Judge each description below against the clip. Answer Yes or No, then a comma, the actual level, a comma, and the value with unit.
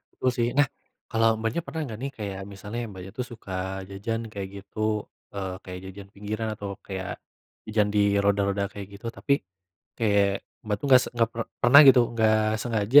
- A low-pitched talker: Yes, low, 105 Hz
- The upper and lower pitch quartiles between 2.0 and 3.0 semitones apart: Yes, narrow, 2.6 semitones